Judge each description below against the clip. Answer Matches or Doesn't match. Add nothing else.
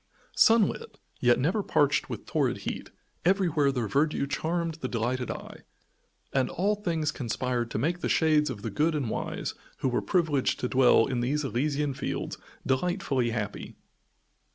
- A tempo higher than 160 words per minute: Doesn't match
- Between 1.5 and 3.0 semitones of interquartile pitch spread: Doesn't match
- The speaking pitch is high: Doesn't match